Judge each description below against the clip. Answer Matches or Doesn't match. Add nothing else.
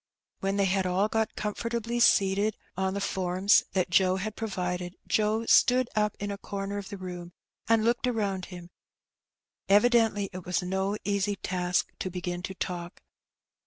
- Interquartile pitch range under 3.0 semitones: Matches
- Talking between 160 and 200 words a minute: Matches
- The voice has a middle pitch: Doesn't match